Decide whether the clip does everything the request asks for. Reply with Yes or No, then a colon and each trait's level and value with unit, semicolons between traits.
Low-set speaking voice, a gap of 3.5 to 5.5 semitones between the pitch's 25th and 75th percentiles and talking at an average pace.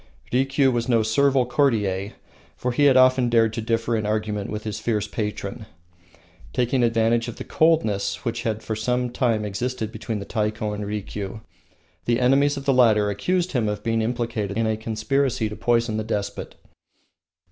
No: low, 115 Hz; average, 2.7 semitones; average, 170 wpm